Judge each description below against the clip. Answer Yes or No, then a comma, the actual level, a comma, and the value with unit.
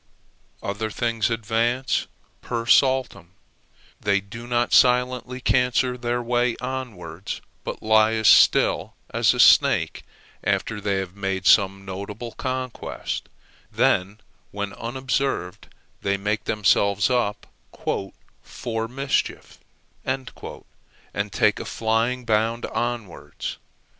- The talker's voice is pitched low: Yes, low, 115 Hz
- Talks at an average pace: No, slow, 105 wpm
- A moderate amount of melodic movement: Yes, average, 3.6 semitones